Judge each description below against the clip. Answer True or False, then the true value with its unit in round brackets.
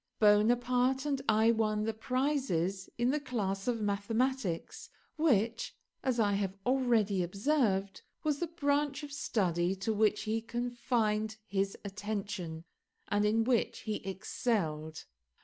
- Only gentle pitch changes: False (4.2 semitones)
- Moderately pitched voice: False (220 Hz)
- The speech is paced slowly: True (130 wpm)